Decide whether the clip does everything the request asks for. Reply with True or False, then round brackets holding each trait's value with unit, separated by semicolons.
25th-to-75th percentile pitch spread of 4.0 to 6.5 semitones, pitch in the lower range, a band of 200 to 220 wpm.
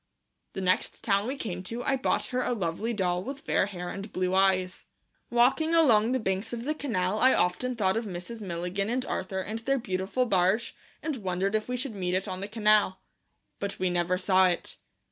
False (4.4 semitones; 200 Hz; 205 wpm)